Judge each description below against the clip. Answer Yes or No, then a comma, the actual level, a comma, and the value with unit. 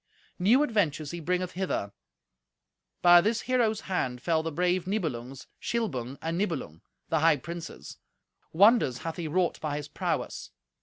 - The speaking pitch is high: No, medium, 170 Hz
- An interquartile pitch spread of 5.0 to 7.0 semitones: No, average, 4.3 semitones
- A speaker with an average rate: Yes, average, 145 wpm